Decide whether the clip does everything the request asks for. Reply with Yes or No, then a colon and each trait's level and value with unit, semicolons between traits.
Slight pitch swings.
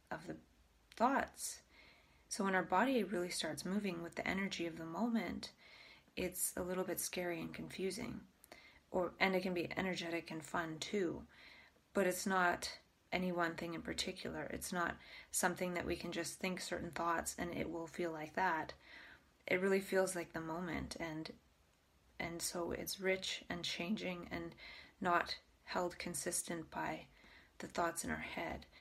Yes: narrow, 2.1 semitones